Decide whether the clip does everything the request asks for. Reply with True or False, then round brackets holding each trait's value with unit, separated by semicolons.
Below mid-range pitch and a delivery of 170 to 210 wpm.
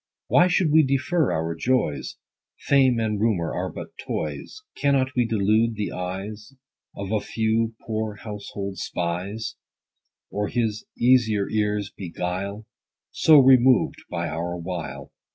False (110 Hz; 135 wpm)